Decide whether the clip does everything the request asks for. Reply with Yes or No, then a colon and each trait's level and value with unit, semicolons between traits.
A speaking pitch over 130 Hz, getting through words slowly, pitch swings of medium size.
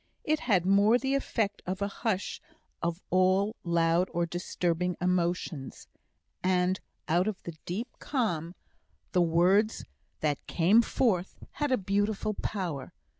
Yes: medium, 185 Hz; slow, 130 wpm; average, 3.5 semitones